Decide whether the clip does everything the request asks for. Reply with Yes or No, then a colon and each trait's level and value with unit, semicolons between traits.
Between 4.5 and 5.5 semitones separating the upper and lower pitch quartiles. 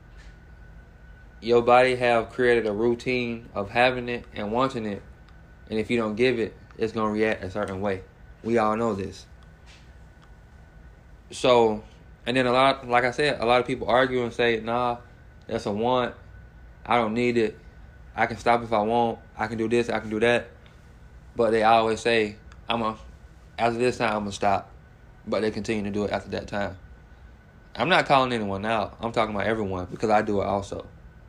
No: average, 3.5 semitones